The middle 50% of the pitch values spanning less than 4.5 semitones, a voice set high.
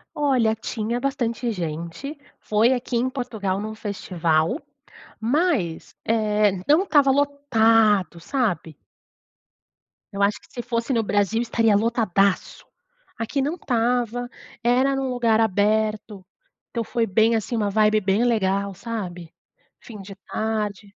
Yes: average, 3.4 semitones; high, 220 Hz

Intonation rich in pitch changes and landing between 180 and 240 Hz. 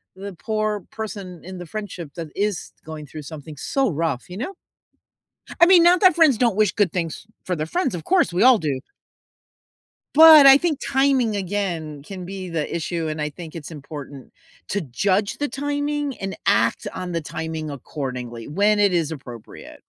Yes: wide, 6.3 semitones; medium, 185 Hz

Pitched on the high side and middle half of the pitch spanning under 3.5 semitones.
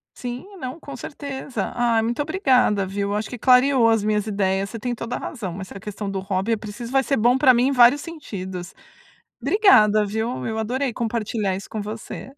No: high, 230 Hz; average, 3.8 semitones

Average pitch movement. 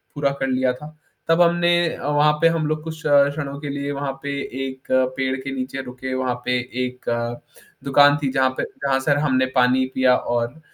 No: narrow, 2.1 semitones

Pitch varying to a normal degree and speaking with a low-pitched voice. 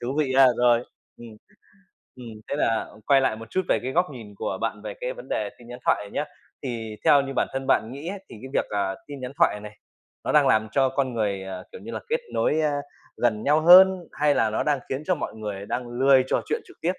Yes: average, 4.9 semitones; low, 130 Hz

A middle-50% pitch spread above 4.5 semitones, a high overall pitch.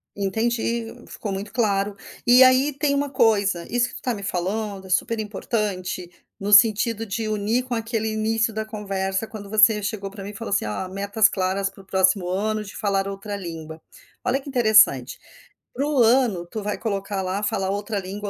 No: narrow, 2.5 semitones; high, 210 Hz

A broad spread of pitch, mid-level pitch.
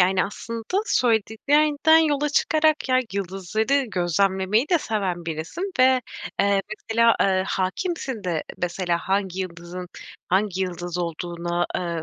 No: wide, 6.4 semitones; high, 195 Hz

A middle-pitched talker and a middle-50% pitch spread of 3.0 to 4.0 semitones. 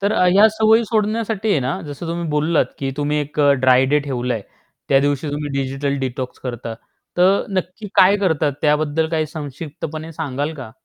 No: medium, 150 Hz; average, 4.8 semitones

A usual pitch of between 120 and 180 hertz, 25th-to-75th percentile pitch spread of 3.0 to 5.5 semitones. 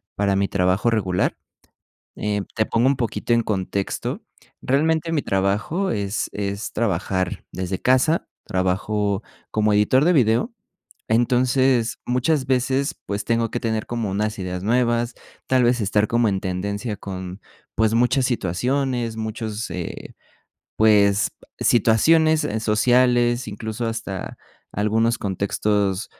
No: low, 110 Hz; average, 3.5 semitones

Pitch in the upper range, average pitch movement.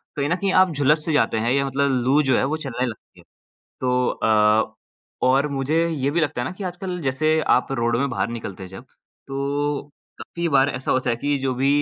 No: low, 135 Hz; average, 3.1 semitones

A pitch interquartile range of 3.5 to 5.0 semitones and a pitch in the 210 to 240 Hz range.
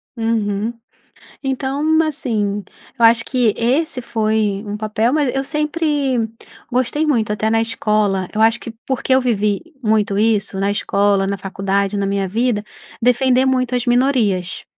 Yes: average, 3.9 semitones; high, 225 Hz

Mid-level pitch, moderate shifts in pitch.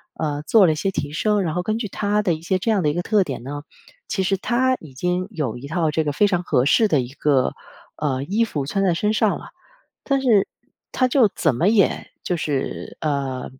No: medium, 175 Hz; wide, 6.1 semitones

